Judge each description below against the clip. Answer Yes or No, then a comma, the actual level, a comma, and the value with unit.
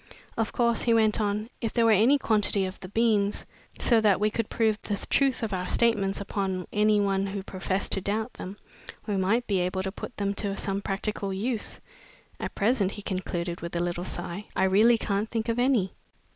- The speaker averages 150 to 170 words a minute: No, fast, 205 wpm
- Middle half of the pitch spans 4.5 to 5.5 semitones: No, average, 2.7 semitones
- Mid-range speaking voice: No, high, 205 Hz